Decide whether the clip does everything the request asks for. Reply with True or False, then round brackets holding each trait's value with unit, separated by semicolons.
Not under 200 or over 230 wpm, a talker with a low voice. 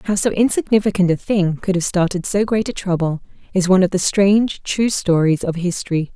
False (205 wpm; 190 Hz)